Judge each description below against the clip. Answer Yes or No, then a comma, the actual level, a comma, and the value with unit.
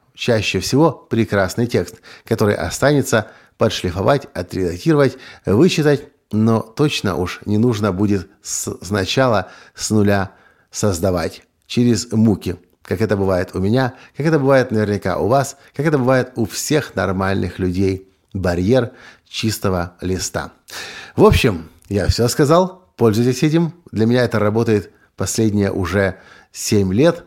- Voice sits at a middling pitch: No, low, 110 Hz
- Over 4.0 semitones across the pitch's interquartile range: Yes, average, 5.2 semitones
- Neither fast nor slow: Yes, average, 125 wpm